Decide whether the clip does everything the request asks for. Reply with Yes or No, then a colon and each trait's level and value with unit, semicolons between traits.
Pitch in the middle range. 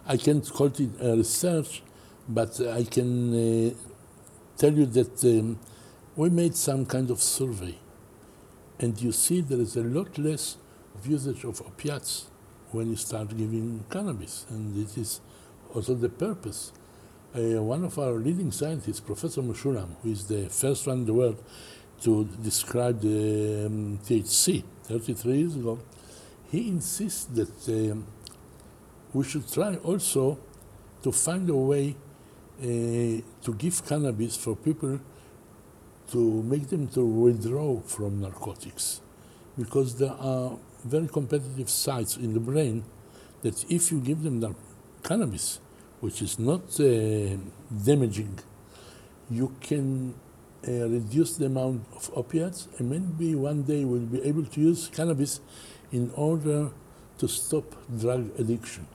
No: low, 120 Hz